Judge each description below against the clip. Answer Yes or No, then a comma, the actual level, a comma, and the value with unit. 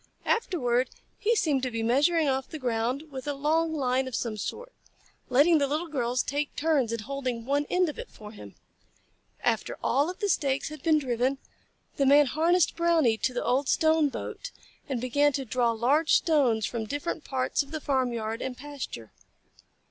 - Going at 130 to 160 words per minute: No, average, 185 wpm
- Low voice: No, very high, 275 Hz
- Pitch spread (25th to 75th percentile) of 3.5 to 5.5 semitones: Yes, average, 3.9 semitones